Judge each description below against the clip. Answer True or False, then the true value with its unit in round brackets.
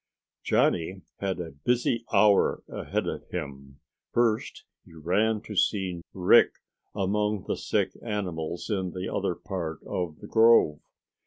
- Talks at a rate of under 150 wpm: True (135 wpm)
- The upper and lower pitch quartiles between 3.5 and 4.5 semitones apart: True (4.2 semitones)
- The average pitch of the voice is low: True (95 Hz)